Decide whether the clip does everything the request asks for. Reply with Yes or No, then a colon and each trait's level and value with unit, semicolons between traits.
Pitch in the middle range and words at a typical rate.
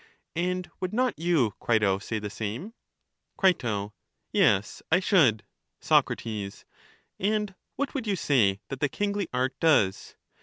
No: medium, 155 Hz; slow, 130 wpm